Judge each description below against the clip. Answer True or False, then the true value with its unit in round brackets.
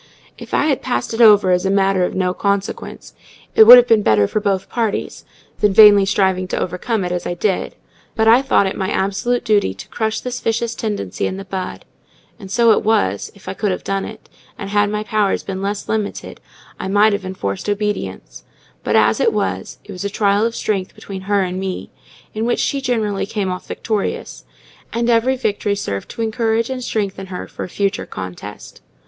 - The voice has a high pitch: True (205 Hz)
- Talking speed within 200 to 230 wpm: True (205 wpm)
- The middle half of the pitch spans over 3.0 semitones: False (2.7 semitones)